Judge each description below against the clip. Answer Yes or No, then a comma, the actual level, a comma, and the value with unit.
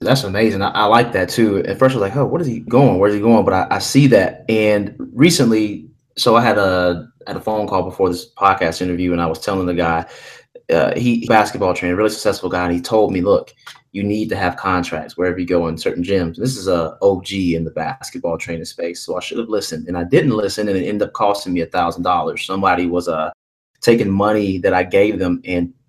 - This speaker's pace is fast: Yes, fast, 245 wpm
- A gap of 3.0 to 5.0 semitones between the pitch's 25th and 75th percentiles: Yes, average, 3.5 semitones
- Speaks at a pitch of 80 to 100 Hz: Yes, very low, 95 Hz